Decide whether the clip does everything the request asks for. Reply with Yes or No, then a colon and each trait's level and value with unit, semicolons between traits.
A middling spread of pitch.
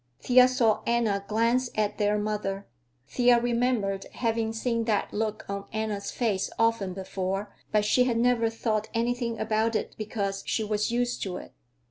No: narrow, 2.3 semitones